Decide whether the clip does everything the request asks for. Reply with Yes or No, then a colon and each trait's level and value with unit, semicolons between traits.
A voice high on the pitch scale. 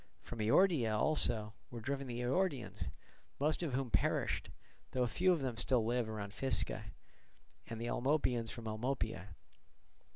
No: low, 120 Hz